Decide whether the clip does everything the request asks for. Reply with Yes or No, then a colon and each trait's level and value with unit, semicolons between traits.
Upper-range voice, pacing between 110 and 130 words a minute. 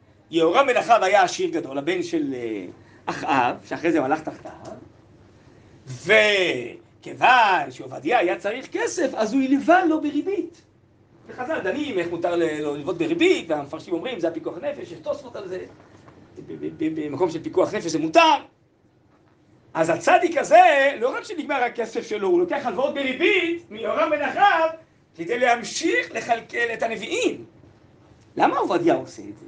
No: very high, 275 Hz; average, 145 wpm